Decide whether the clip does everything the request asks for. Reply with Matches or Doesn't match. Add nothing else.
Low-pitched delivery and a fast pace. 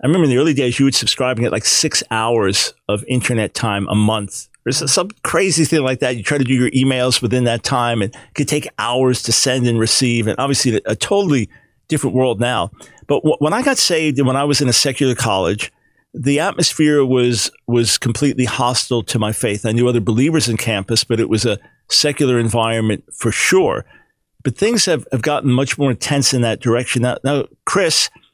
Matches